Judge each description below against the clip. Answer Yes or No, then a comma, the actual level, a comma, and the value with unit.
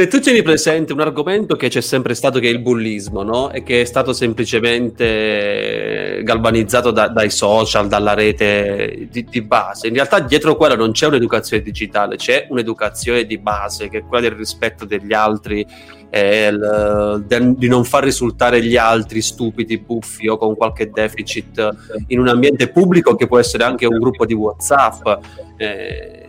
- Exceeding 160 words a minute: Yes, fast, 170 wpm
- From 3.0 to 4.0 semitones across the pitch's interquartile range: No, narrow, 2.5 semitones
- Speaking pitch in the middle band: No, low, 115 Hz